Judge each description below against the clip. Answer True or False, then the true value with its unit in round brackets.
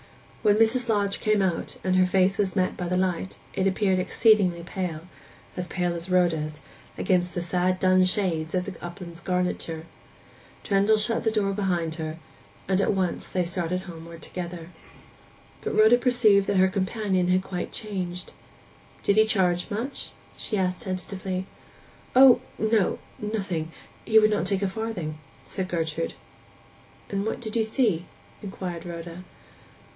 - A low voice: False (185 Hz)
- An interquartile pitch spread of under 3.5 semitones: True (2.8 semitones)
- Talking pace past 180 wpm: False (150 wpm)